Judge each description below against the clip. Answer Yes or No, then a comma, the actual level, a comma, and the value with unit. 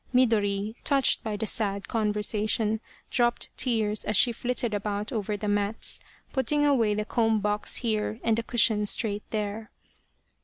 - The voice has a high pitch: Yes, high, 215 Hz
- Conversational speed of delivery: Yes, average, 150 wpm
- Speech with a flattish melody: Yes, narrow, 1.9 semitones